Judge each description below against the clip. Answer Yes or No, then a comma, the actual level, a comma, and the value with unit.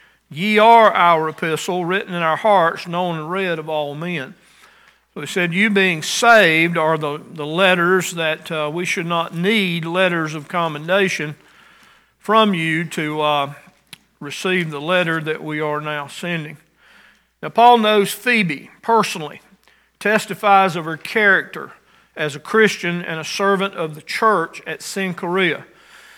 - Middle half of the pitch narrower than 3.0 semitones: No, average, 3.7 semitones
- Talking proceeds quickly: No, average, 150 wpm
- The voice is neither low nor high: Yes, medium, 175 Hz